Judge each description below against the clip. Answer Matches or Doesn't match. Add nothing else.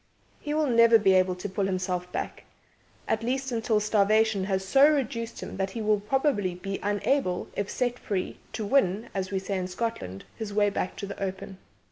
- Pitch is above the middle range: Matches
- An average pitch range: Matches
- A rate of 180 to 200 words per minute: Matches